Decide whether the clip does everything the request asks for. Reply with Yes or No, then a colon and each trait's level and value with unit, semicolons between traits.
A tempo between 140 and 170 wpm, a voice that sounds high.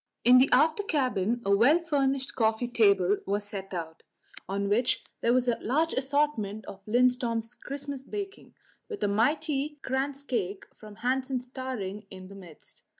Yes: average, 150 wpm; high, 245 Hz